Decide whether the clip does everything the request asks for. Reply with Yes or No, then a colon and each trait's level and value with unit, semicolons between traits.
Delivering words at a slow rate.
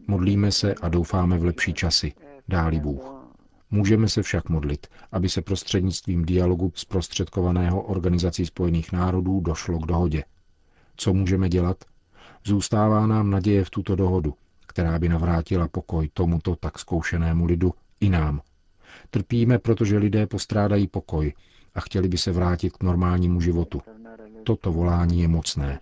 No: average, 140 wpm